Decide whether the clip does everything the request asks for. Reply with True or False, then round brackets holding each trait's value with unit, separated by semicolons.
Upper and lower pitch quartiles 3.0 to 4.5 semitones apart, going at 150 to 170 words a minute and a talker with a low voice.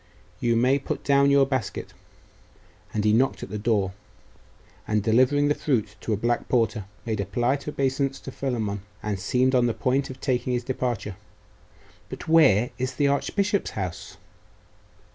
True (4.2 semitones; 160 wpm; 125 Hz)